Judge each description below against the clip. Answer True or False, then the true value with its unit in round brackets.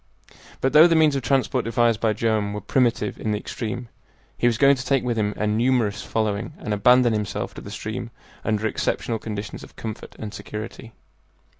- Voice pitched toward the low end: True (115 Hz)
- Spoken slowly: False (190 wpm)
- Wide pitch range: False (2.8 semitones)